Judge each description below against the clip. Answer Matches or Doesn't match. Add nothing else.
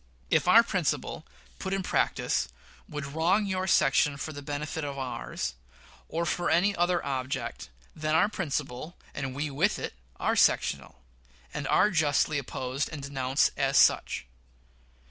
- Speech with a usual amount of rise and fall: Matches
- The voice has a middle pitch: Matches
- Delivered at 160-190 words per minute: Doesn't match